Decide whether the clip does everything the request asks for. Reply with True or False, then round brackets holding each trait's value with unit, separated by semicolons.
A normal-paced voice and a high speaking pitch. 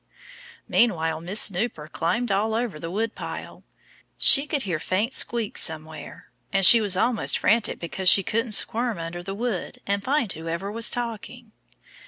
True (155 wpm; 205 Hz)